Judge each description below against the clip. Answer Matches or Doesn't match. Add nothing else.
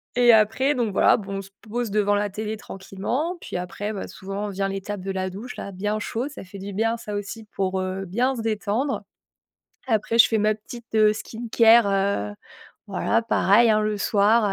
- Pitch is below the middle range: Doesn't match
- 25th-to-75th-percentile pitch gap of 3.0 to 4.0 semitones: Doesn't match